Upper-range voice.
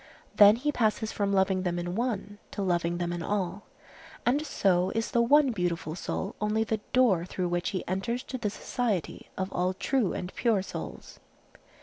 Yes: high, 200 Hz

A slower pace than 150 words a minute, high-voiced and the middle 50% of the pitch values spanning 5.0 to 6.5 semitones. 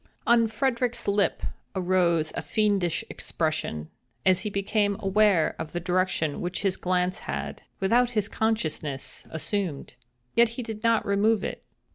No: average, 140 wpm; high, 195 Hz; average, 4.3 semitones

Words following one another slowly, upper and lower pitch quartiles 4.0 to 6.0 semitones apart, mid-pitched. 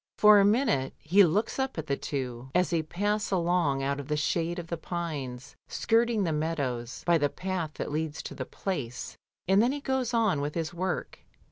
No: fast, 205 wpm; wide, 5.6 semitones; medium, 170 Hz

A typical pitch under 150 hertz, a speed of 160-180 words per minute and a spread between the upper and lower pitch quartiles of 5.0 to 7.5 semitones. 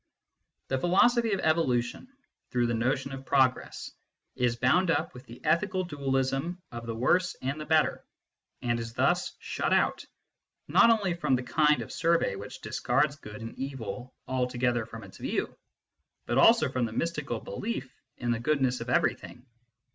Yes: low, 135 Hz; average, 165 wpm; average, 5.3 semitones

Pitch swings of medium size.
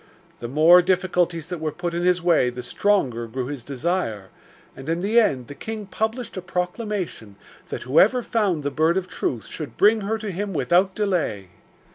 No: wide, 6.0 semitones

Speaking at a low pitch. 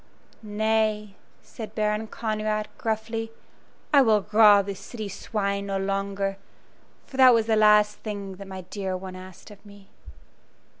No: high, 210 Hz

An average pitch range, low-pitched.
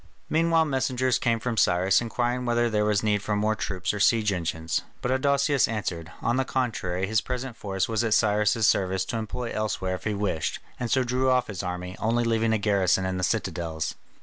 Yes: average, 4.3 semitones; low, 110 Hz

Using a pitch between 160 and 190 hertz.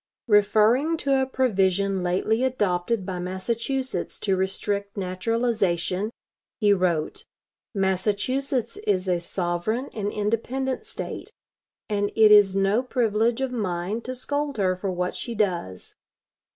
No: high, 205 Hz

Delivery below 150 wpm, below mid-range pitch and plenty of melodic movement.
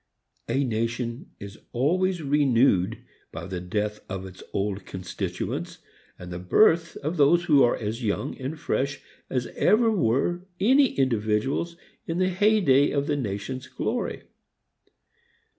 Yes: average, 140 wpm; low, 130 Hz; wide, 7.7 semitones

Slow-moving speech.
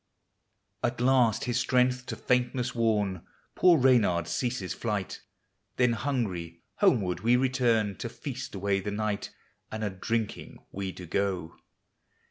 Yes: slow, 130 wpm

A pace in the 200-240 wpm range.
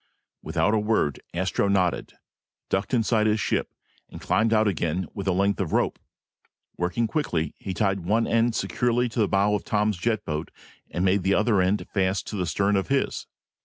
No: average, 190 wpm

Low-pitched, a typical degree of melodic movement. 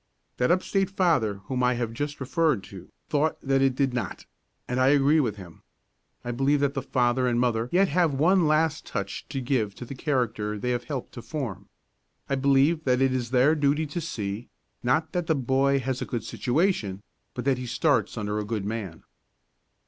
Yes: low, 130 Hz; average, 3.7 semitones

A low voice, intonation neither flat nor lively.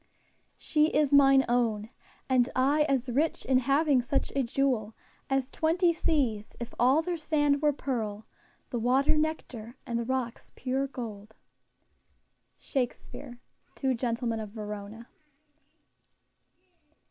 No: very high, 260 Hz; average, 3.4 semitones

